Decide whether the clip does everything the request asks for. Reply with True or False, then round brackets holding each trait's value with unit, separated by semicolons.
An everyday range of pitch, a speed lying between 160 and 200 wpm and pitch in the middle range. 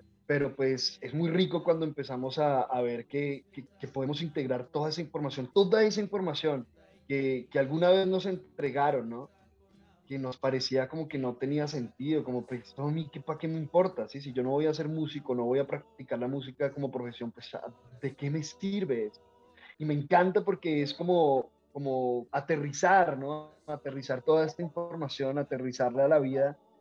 True (3.3 semitones; 185 wpm; 145 Hz)